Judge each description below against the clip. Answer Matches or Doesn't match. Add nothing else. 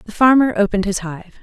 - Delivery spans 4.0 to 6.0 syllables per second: Doesn't match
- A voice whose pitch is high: Matches